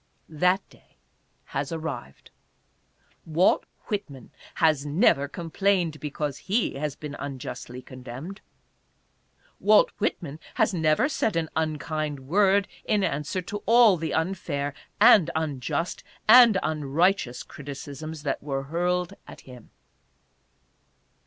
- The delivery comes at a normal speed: No, slow, 115 wpm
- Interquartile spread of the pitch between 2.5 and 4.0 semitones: No, average, 4.7 semitones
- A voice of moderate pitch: Yes, medium, 155 Hz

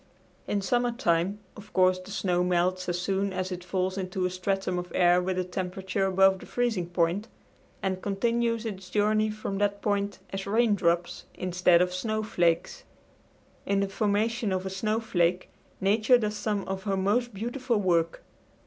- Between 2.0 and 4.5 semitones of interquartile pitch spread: Yes, average, 2.7 semitones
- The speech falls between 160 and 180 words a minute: Yes, average, 165 wpm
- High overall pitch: Yes, high, 195 Hz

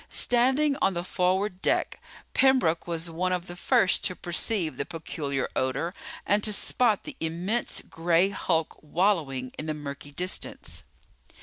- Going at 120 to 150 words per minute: Yes, average, 145 wpm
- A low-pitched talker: No, medium, 175 Hz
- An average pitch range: Yes, average, 3.9 semitones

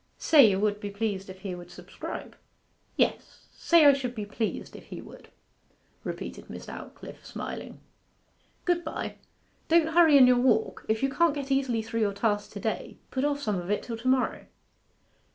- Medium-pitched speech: No, high, 240 Hz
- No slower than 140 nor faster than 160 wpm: No, average, 185 wpm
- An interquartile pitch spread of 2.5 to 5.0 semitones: No, wide, 5.4 semitones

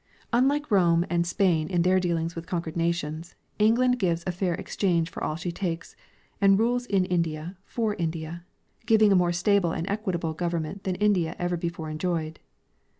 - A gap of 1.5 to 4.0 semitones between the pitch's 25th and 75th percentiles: Yes, average, 2.9 semitones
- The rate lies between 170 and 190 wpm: Yes, average, 175 wpm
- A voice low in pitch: No, medium, 175 Hz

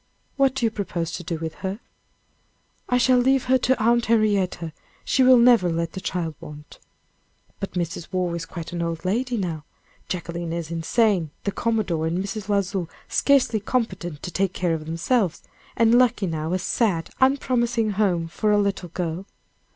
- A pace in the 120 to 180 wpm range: Yes, average, 170 wpm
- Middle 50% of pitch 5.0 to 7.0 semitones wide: Yes, wide, 5.6 semitones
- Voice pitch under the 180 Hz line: No, high, 190 Hz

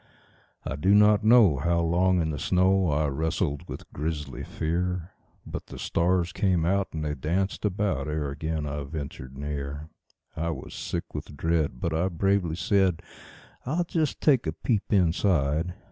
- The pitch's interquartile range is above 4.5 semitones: No, average, 4.2 semitones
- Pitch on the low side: Yes, very low, 85 Hz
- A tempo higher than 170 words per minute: No, average, 160 wpm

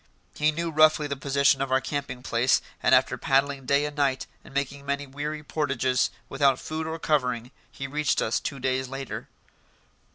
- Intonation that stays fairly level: Yes, narrow, 2.0 semitones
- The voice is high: No, medium, 140 Hz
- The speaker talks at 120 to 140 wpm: No, average, 175 wpm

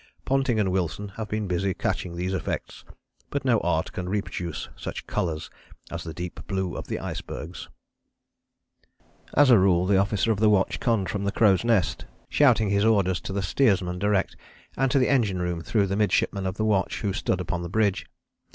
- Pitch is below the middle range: Yes, low, 100 Hz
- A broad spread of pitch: No, average, 3.3 semitones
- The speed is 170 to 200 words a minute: Yes, average, 190 wpm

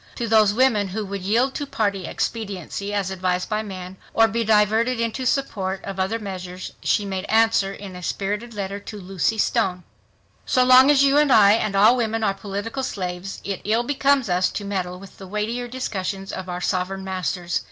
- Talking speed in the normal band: Yes, average, 195 wpm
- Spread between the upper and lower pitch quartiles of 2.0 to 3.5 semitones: Yes, average, 3.2 semitones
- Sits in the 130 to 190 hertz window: No, high, 205 Hz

